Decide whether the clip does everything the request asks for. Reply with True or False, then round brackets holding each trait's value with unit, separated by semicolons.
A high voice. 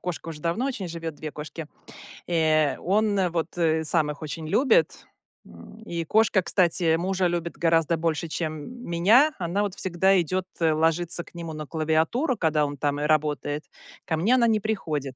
False (165 Hz)